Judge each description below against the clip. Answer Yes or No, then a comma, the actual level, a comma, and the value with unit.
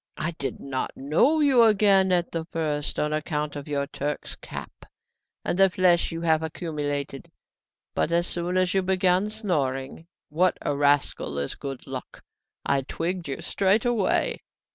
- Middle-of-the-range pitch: Yes, medium, 165 Hz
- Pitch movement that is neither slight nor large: Yes, average, 4.4 semitones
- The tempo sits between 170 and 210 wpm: No, average, 160 wpm